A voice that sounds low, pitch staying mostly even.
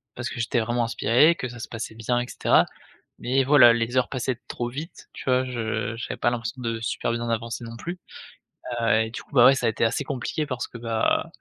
Yes: low, 120 Hz; narrow, 1.9 semitones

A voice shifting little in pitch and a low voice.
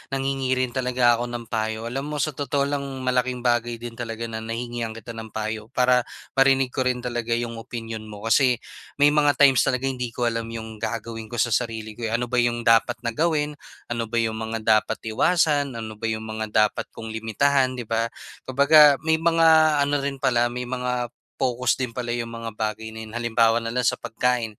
Yes: narrow, 2.2 semitones; low, 120 Hz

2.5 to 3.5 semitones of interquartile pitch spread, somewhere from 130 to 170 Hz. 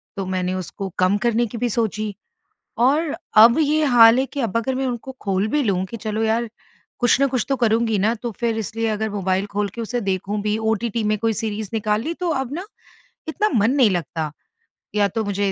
No: average, 2.9 semitones; high, 225 Hz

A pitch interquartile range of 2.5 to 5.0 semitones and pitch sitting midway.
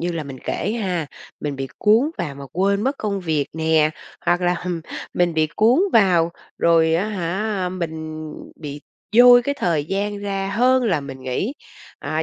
Yes: average, 4.6 semitones; medium, 175 Hz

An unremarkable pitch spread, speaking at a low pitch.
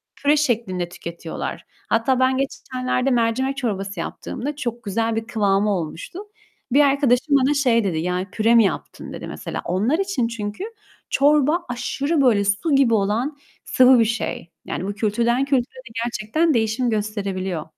No: average, 4.8 semitones; high, 235 Hz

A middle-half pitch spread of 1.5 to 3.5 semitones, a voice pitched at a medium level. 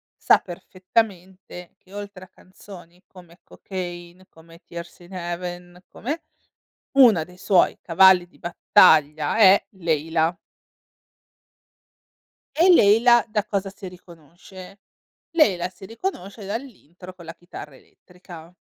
Yes: narrow, 2.4 semitones; medium, 180 Hz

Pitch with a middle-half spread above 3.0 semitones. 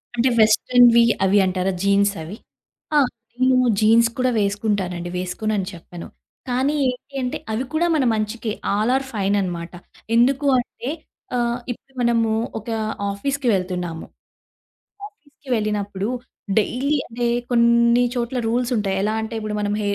Yes: average, 3.6 semitones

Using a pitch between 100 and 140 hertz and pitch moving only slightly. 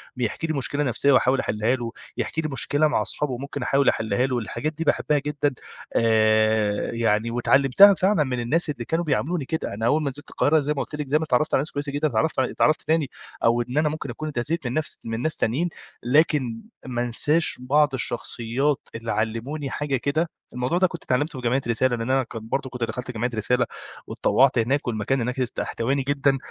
No: low, 135 Hz; average, 3.8 semitones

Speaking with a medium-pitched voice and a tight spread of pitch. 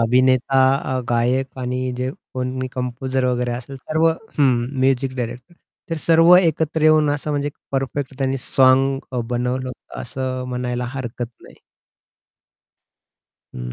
No: low, 130 Hz; narrow, 1.8 semitones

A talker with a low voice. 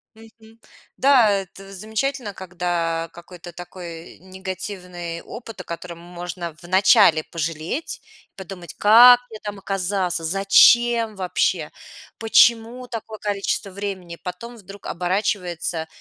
No: high, 190 Hz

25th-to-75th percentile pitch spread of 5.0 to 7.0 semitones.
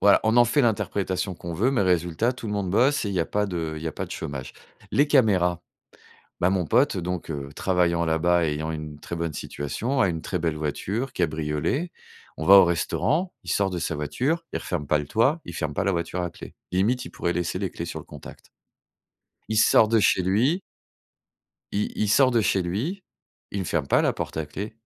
Yes: average, 5.3 semitones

